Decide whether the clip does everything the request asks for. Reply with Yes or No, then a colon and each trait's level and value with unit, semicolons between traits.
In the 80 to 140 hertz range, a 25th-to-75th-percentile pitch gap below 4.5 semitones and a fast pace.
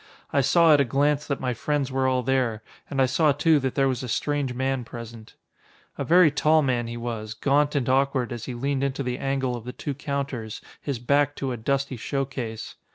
Yes: low, 135 Hz; narrow, 2.4 semitones; fast, 225 wpm